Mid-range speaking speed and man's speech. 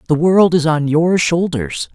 Yes: average, 185 wpm; male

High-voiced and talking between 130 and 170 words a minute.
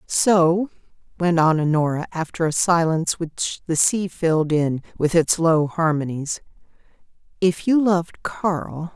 No: medium, 165 Hz; slow, 135 wpm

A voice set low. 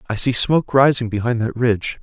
Yes: low, 120 Hz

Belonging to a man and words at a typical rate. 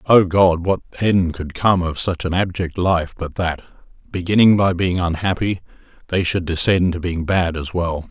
Yes: male; average, 185 wpm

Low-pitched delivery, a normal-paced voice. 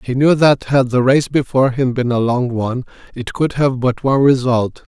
No: low, 130 Hz; fast, 220 wpm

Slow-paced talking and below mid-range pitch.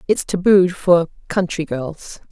No: slow, 105 wpm; medium, 175 Hz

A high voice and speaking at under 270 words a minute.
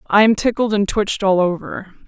Yes: high, 200 Hz; fast, 205 wpm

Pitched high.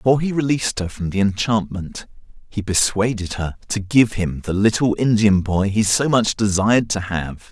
No: low, 105 Hz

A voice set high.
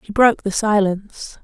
Yes: high, 205 Hz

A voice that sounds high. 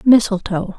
Yes: high, 205 Hz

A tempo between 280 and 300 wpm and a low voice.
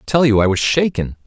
Yes: fast, 285 wpm; low, 120 Hz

